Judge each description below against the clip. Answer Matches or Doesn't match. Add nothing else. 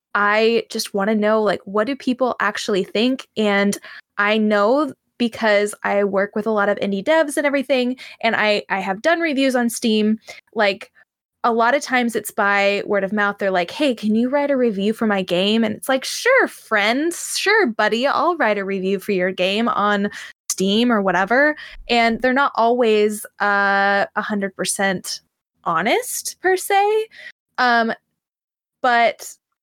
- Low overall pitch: Doesn't match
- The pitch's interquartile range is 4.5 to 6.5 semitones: Matches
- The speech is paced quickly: Doesn't match